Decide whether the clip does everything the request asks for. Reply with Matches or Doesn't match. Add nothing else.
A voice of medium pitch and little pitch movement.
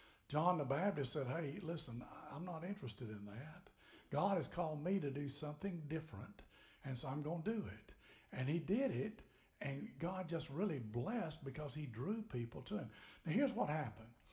Doesn't match